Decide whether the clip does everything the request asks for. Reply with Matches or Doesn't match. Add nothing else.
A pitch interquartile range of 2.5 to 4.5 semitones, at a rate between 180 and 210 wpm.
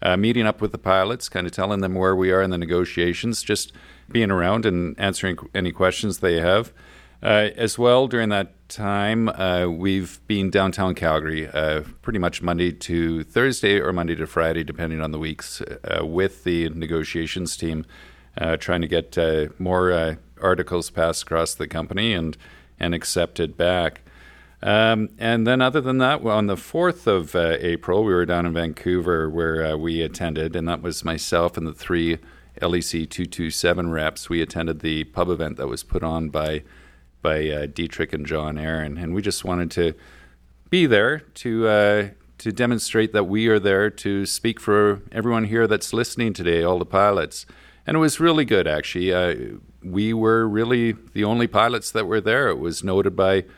Matches